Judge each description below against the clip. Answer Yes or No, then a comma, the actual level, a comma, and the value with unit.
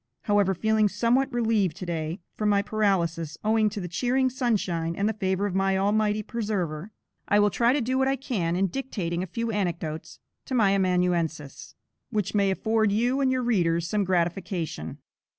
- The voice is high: Yes, high, 200 Hz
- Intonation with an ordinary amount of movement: Yes, average, 4.2 semitones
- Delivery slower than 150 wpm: No, average, 180 wpm